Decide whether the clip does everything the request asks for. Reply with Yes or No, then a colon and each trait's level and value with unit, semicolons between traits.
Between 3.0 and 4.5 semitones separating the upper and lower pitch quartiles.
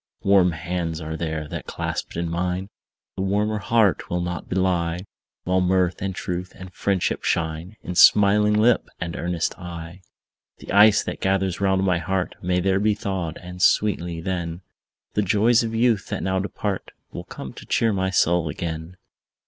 No: narrow, 2.6 semitones